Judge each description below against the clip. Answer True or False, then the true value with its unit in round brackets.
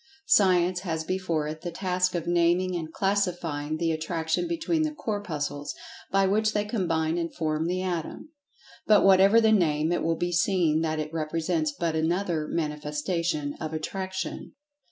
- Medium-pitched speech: True (170 Hz)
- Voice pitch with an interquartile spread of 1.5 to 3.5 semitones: True (3.1 semitones)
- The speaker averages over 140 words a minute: True (155 wpm)